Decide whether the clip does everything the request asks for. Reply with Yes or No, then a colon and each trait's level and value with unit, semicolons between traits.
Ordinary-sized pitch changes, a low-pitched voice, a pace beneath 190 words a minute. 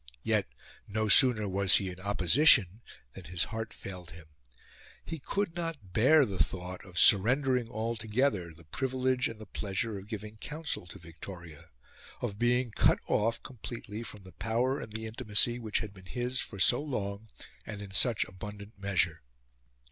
Yes: average, 4.2 semitones; low, 105 Hz; average, 165 wpm